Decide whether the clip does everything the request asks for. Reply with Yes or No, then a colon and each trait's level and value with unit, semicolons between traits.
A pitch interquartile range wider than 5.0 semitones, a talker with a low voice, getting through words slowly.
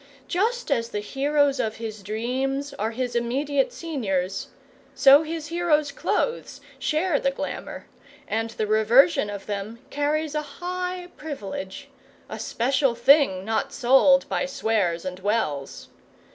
No: wide, 5.5 semitones; very high, 270 Hz; slow, 130 wpm